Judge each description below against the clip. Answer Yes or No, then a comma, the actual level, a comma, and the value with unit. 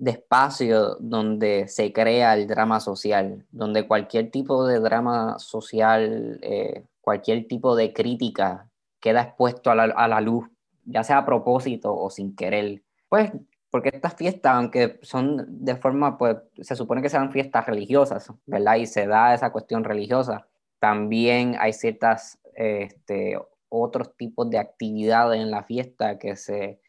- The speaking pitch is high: No, low, 115 Hz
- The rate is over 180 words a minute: No, average, 155 wpm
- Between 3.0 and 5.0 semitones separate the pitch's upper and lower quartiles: No, narrow, 2.5 semitones